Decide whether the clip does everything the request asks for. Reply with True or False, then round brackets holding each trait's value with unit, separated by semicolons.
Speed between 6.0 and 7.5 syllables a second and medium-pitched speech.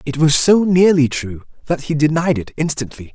False (5.1 syllables/s; 150 Hz)